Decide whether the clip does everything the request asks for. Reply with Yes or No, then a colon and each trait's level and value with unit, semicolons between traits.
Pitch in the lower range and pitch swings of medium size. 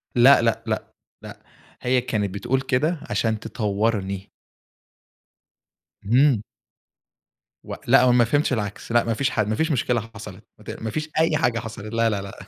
Yes: low, 115 Hz; average, 3.1 semitones